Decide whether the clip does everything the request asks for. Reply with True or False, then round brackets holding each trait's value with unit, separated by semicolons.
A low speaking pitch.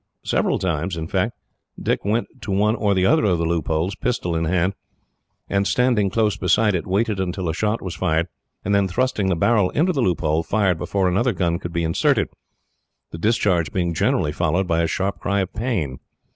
True (95 Hz)